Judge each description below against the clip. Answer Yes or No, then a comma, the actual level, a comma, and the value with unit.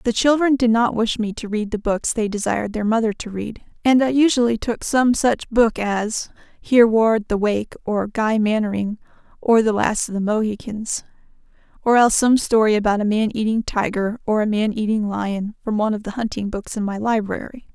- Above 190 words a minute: Yes, average, 200 wpm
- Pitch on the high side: Yes, high, 220 Hz